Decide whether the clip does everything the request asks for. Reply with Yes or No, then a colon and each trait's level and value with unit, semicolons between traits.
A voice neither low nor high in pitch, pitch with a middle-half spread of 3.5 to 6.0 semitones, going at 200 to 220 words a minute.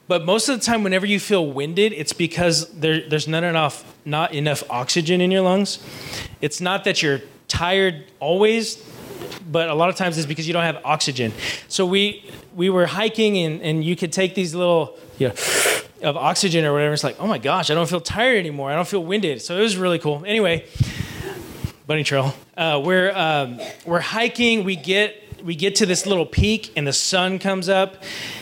Yes: medium, 175 Hz; average, 4.3 semitones; fast, 205 wpm